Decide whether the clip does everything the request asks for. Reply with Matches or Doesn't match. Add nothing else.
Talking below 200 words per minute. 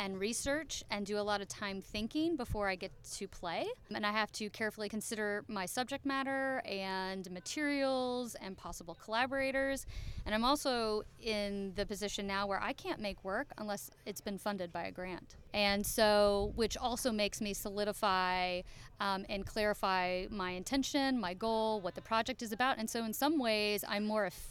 Matches